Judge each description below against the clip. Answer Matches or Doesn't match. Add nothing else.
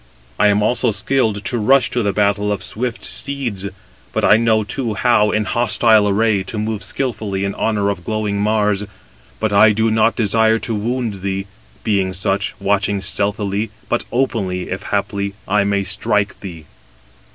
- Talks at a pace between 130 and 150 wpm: Doesn't match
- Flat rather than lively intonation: Matches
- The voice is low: Matches